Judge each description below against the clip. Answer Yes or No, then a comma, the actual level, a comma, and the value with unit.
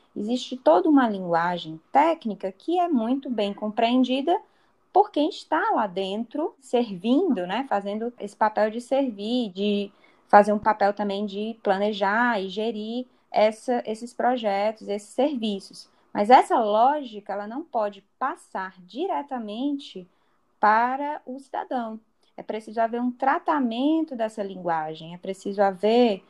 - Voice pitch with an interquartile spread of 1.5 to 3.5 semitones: No, average, 4.5 semitones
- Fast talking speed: No, average, 130 wpm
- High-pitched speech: Yes, high, 225 Hz